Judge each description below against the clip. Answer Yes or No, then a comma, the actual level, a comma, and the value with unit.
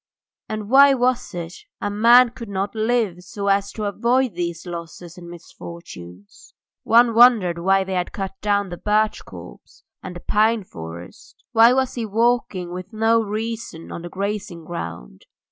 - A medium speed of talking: Yes, average, 160 wpm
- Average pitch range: Yes, average, 4.7 semitones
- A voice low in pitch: No, high, 200 Hz